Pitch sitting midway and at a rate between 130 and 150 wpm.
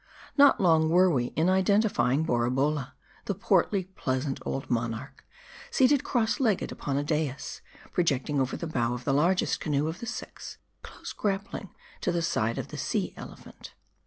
No: medium, 160 Hz; average, 165 wpm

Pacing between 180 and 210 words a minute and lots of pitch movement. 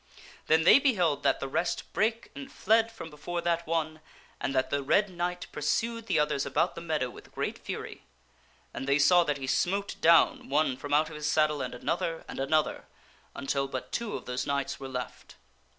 No: average, 200 wpm; average, 4.2 semitones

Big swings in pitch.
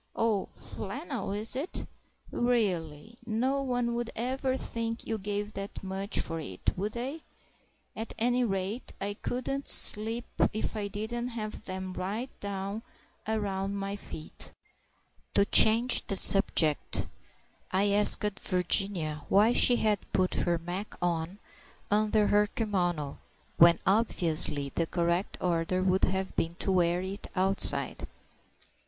No: average, 3.6 semitones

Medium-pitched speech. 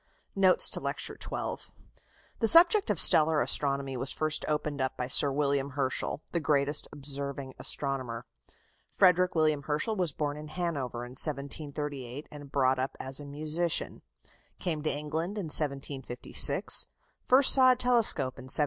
Yes: medium, 145 Hz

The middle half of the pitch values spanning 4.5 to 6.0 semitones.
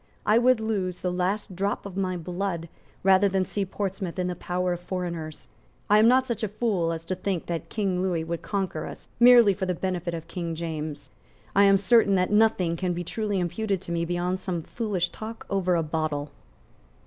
No: average, 2.8 semitones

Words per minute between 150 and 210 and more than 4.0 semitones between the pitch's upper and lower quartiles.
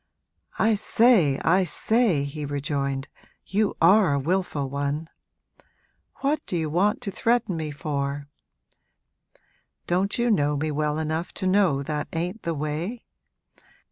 No: slow, 135 wpm; wide, 5.5 semitones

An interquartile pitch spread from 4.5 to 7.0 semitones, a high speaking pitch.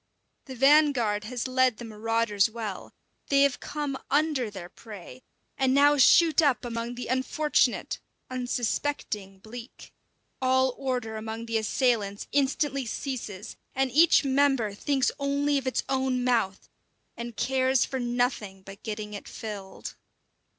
No: average, 3.8 semitones; very high, 250 Hz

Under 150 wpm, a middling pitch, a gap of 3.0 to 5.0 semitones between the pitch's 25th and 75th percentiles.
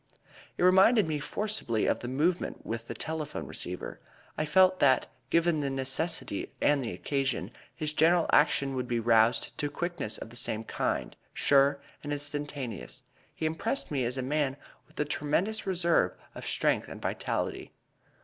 No: average, 160 wpm; medium, 145 Hz; average, 4.4 semitones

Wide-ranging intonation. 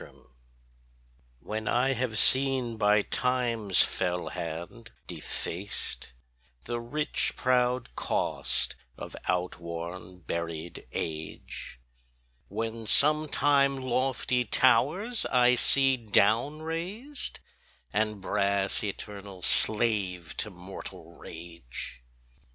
Yes: wide, 5.9 semitones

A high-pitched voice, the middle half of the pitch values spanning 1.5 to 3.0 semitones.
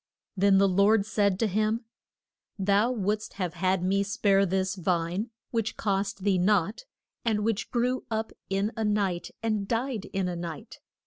Yes: high, 200 Hz; narrow, 2.5 semitones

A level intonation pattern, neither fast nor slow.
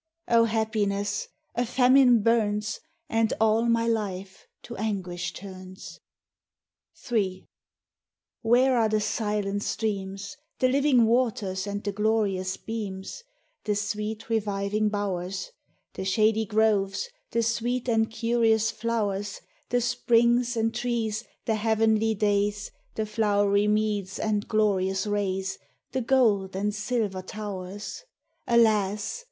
No: narrow, 2.3 semitones; slow, 115 wpm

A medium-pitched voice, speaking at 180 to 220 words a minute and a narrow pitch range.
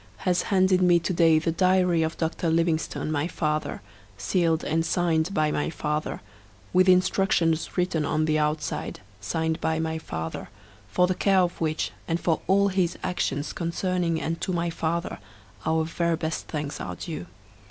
No: medium, 165 Hz; average, 170 wpm; narrow, 2.2 semitones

